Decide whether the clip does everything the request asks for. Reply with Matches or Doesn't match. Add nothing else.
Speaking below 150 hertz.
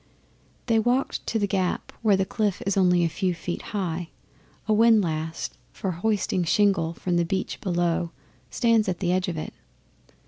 Doesn't match